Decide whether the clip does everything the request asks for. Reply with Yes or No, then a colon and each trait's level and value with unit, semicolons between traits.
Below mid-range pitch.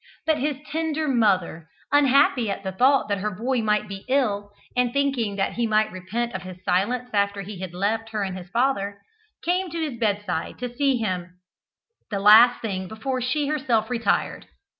No: high, 220 Hz